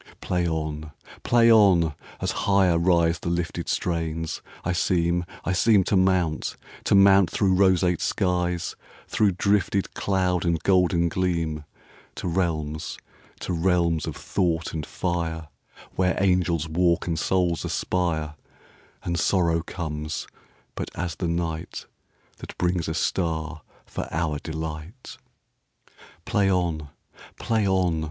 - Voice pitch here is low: Yes, very low, 85 Hz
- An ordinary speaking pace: No, slow, 110 wpm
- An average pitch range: No, narrow, 2.2 semitones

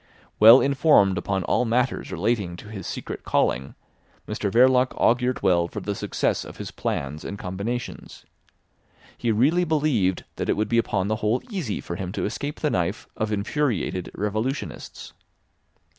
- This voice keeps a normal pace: Yes, average, 160 wpm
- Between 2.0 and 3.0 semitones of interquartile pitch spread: No, average, 4.9 semitones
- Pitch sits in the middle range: No, low, 110 Hz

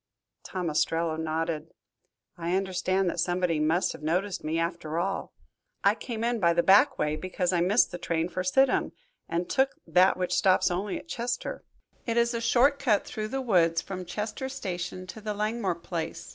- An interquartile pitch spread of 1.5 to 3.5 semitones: No, average, 4.2 semitones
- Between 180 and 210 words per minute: Yes, average, 185 wpm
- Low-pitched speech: No, medium, 185 Hz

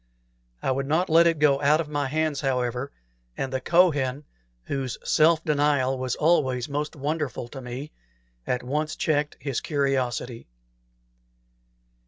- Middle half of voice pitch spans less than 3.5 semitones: Yes, average, 2.8 semitones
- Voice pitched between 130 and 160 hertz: Yes, medium, 140 Hz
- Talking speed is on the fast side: No, average, 145 wpm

